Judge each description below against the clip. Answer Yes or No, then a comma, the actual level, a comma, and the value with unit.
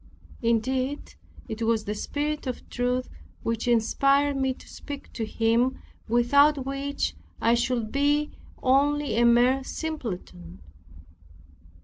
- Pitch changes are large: No, average, 3.5 semitones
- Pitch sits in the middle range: No, very high, 255 Hz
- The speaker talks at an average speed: No, slow, 115 wpm